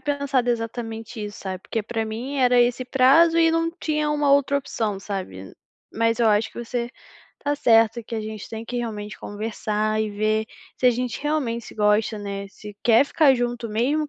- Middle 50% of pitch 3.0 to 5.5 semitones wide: Yes, average, 3.7 semitones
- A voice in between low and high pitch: No, high, 230 Hz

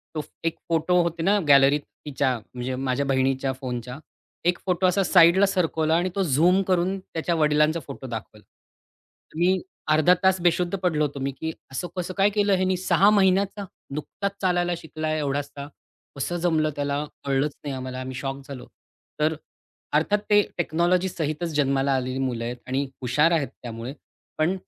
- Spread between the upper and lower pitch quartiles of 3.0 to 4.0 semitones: No, average, 4.8 semitones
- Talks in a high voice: No, medium, 155 Hz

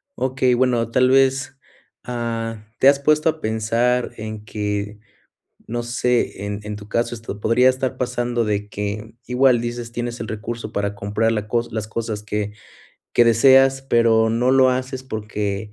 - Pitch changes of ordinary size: Yes, average, 3.0 semitones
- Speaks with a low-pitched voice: Yes, low, 115 Hz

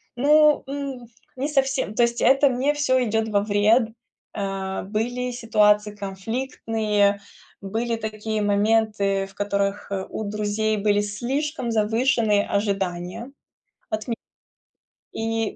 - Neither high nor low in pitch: No, high, 220 Hz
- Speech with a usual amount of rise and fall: Yes, average, 3.2 semitones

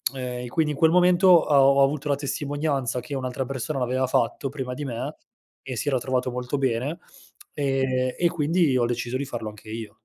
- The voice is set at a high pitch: No, low, 135 Hz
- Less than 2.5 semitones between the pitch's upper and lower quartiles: No, average, 2.8 semitones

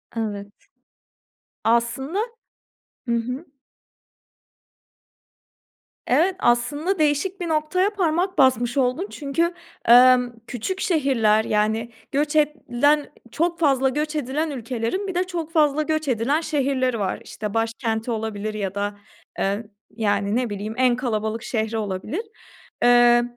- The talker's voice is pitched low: No, very high, 255 Hz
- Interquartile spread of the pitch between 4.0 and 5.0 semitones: No, wide, 5.4 semitones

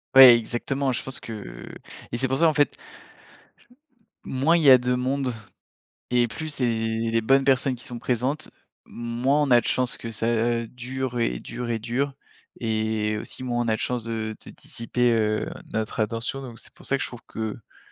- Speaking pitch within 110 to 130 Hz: Yes, low, 120 Hz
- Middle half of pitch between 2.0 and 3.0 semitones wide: Yes, average, 2.7 semitones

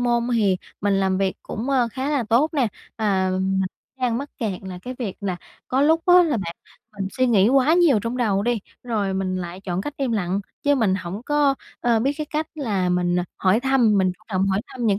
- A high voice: Yes, high, 220 Hz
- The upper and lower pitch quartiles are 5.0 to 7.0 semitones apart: Yes, average, 5.3 semitones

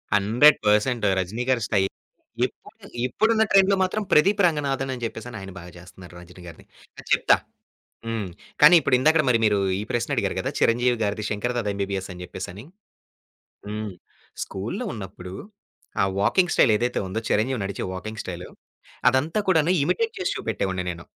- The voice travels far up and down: Yes, wide, 5.9 semitones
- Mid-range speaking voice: No, low, 110 Hz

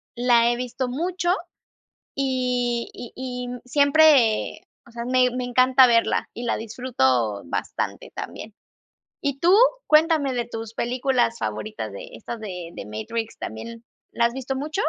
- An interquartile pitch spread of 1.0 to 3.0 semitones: Yes, narrow, 2.5 semitones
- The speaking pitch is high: Yes, high, 245 Hz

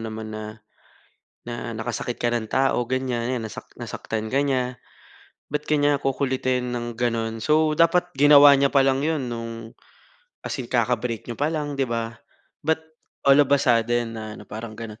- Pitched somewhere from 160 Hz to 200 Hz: No, low, 125 Hz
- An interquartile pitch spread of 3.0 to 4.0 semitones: Yes, average, 3.5 semitones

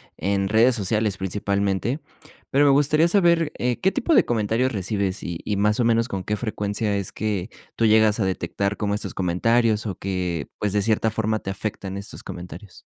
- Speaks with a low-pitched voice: Yes, low, 105 Hz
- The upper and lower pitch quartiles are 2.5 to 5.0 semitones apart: Yes, average, 2.9 semitones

